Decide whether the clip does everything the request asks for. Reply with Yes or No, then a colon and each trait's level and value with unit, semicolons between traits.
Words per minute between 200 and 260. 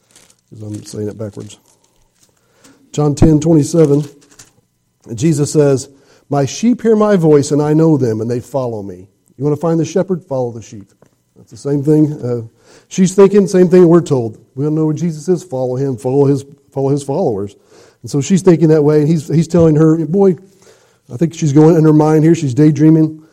Yes: fast, 205 wpm